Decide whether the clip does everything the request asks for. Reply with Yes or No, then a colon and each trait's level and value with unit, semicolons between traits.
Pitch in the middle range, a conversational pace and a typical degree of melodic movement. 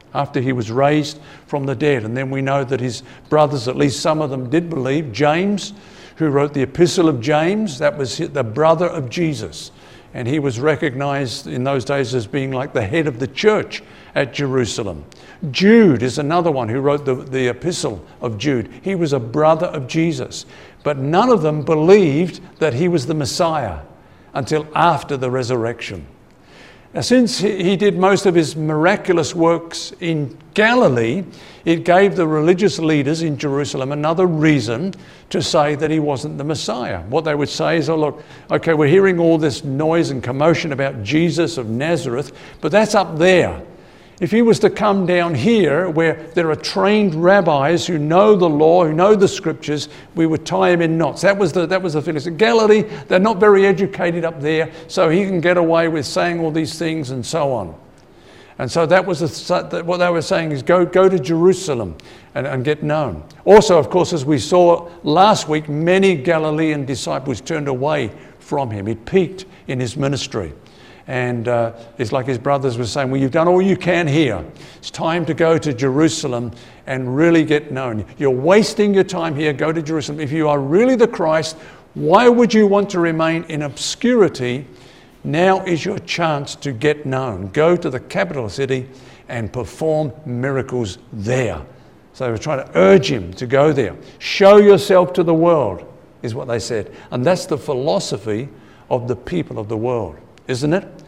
Yes: medium, 155 Hz; average, 190 wpm; average, 4.4 semitones